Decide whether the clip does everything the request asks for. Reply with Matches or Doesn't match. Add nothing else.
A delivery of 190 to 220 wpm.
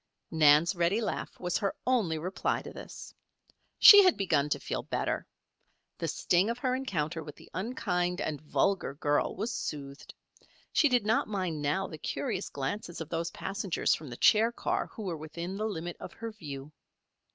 Doesn't match